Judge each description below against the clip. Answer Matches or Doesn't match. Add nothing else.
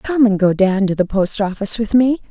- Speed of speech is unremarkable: Doesn't match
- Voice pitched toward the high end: Matches